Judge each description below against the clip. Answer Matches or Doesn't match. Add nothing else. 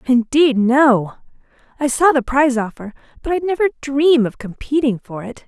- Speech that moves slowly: Doesn't match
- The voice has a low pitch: Doesn't match